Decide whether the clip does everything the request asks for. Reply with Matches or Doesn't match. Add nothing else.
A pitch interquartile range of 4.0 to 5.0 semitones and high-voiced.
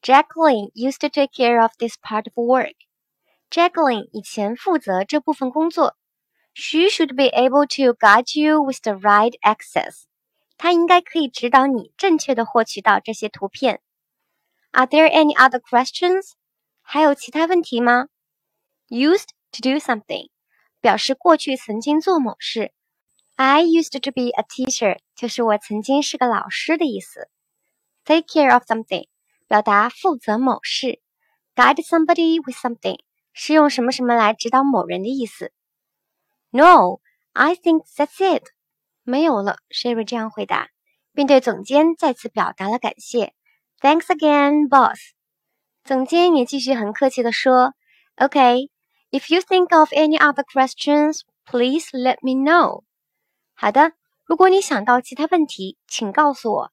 Matches